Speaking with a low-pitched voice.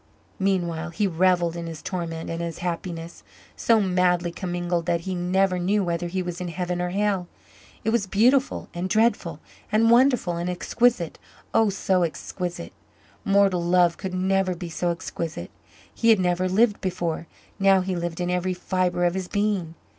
No: medium, 180 Hz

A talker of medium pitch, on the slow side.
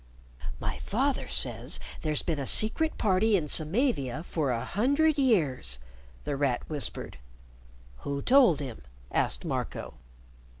Yes: medium, 160 Hz; slow, 125 wpm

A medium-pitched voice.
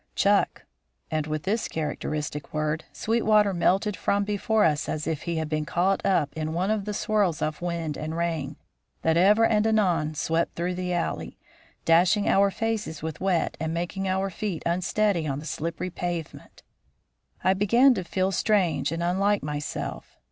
Yes: medium, 175 Hz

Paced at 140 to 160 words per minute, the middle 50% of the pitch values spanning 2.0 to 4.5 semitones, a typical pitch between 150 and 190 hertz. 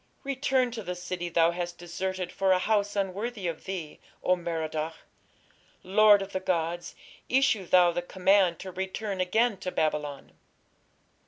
Yes: average, 150 wpm; average, 2.7 semitones; medium, 185 Hz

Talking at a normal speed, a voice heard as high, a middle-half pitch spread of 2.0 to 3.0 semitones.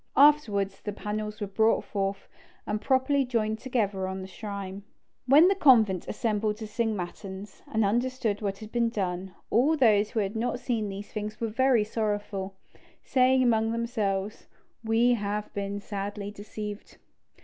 Yes: average, 150 wpm; high, 215 Hz; average, 2.7 semitones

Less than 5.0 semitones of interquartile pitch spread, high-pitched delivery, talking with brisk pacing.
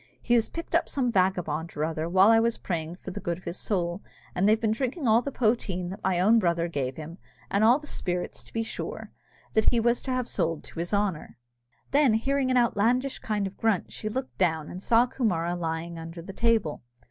No: wide, 5.4 semitones; high, 200 Hz; fast, 230 wpm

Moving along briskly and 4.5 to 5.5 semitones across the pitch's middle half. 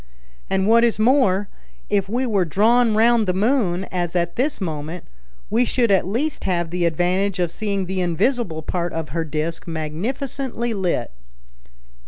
No: average, 160 wpm; average, 5.1 semitones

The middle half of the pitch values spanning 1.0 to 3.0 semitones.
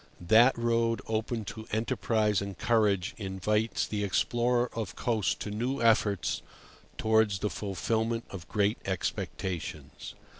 Yes: narrow, 2.5 semitones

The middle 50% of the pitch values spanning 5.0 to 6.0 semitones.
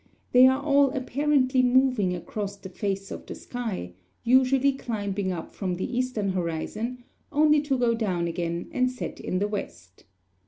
Yes: wide, 5.5 semitones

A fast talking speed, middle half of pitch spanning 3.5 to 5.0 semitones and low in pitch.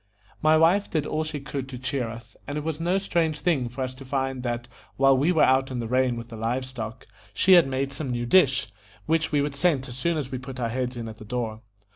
Yes: fast, 260 wpm; average, 3.8 semitones; low, 130 Hz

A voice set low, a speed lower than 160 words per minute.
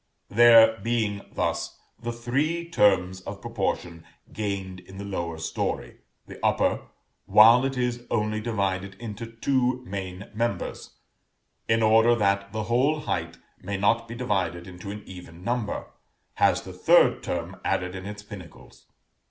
Yes: low, 105 Hz; average, 145 wpm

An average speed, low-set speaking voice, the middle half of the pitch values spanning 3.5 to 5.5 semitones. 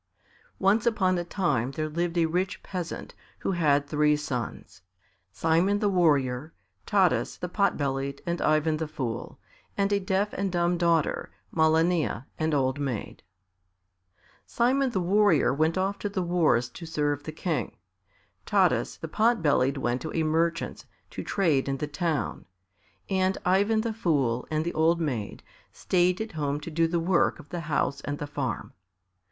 No: average, 165 wpm; medium, 165 Hz; average, 4.3 semitones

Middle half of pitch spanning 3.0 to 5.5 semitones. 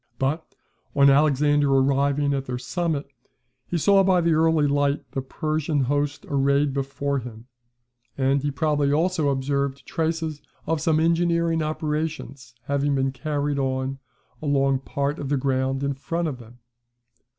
No: narrow, 2.4 semitones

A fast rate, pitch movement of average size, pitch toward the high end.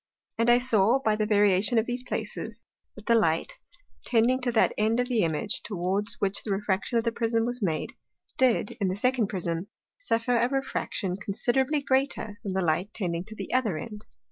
No: average, 195 wpm; average, 3.9 semitones; high, 220 Hz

